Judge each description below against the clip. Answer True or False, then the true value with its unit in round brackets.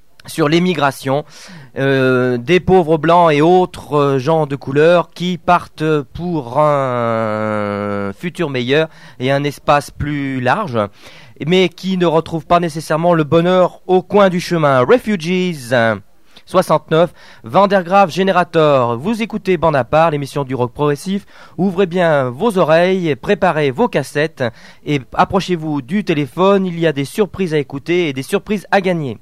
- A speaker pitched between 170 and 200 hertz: False (160 Hz)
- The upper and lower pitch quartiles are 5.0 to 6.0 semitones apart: False (4.6 semitones)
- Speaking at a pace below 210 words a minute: True (145 wpm)